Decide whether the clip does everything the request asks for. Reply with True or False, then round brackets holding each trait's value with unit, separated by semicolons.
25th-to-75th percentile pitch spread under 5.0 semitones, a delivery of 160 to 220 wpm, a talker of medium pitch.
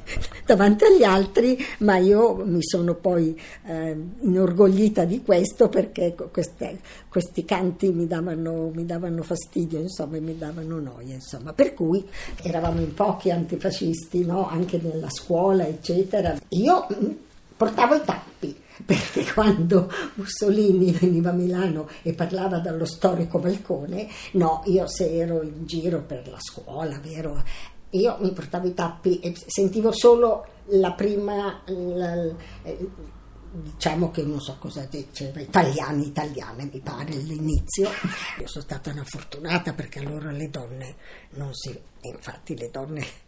False (3.3 semitones; 140 wpm; 170 Hz)